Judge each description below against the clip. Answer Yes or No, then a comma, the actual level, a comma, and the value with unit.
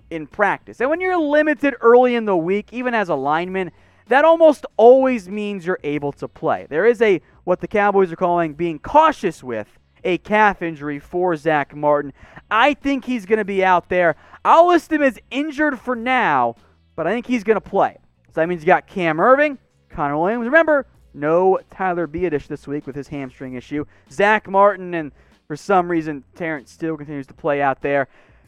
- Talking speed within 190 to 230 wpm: Yes, average, 195 wpm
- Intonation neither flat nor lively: No, wide, 8.3 semitones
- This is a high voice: No, medium, 180 Hz